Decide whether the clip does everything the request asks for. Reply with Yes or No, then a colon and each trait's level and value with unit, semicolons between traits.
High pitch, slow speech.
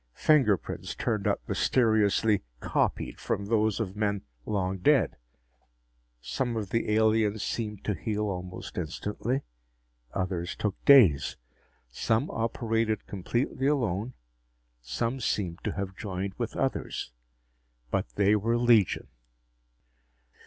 No: low, 105 Hz; slow, 110 wpm